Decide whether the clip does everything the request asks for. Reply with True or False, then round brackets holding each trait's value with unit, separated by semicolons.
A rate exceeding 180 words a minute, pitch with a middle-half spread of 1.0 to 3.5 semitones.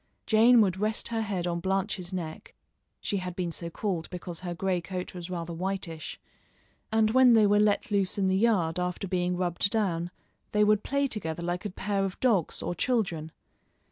True (190 wpm; 3.2 semitones)